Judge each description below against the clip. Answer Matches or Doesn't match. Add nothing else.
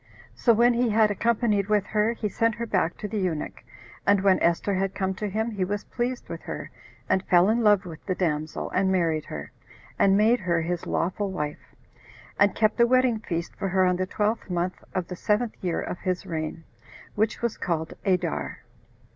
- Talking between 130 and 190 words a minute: Doesn't match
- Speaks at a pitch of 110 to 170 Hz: Doesn't match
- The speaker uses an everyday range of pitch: Matches